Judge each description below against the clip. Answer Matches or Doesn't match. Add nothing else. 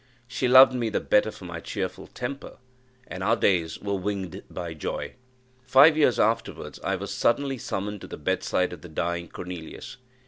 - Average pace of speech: Matches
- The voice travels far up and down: Matches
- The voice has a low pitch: Matches